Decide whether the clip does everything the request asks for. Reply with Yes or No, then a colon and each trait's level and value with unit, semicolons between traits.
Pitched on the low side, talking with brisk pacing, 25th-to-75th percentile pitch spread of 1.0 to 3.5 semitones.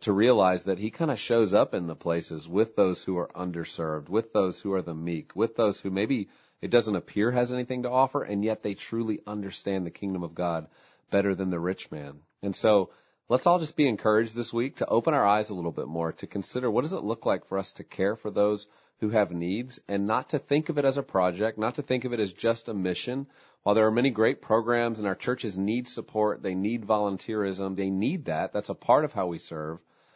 No: low, 105 Hz; fast, 245 wpm; average, 3.9 semitones